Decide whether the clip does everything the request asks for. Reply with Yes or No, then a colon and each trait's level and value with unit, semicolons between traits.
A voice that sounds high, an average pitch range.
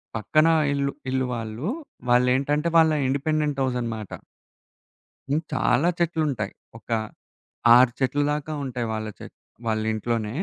No: low, 130 Hz; average, 4.2 semitones